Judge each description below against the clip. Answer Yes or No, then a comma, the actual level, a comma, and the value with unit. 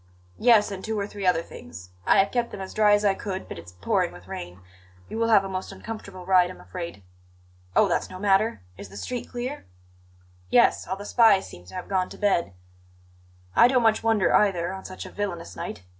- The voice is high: Yes, high, 195 Hz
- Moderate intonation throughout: Yes, average, 3.9 semitones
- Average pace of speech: No, fast, 220 wpm